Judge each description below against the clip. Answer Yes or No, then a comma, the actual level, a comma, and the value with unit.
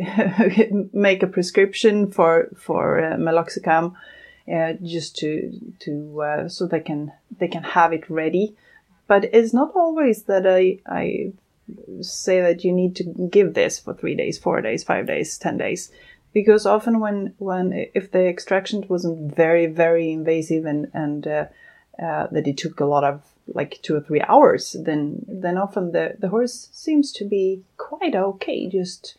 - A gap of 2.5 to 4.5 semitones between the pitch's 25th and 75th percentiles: Yes, average, 3.9 semitones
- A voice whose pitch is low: No, medium, 185 Hz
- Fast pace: No, average, 165 wpm